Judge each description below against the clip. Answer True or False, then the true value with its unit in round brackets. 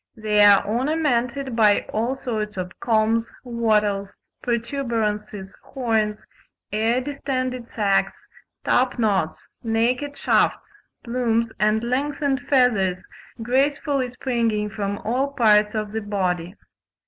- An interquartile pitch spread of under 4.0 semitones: True (3.2 semitones)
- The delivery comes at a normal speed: False (105 wpm)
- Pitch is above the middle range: True (230 Hz)